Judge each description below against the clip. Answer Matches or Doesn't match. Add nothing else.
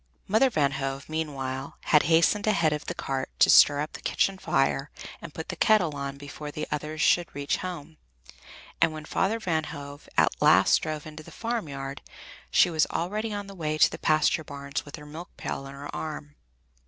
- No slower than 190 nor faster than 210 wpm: Matches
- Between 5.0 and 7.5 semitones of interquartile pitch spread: Doesn't match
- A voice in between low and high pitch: Matches